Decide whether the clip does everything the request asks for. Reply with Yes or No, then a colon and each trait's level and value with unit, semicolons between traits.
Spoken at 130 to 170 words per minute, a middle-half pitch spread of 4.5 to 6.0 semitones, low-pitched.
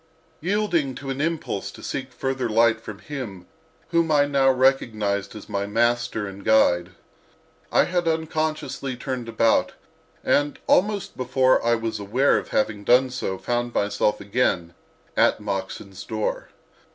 Yes: average, 140 wpm; average, 4.9 semitones; low, 120 Hz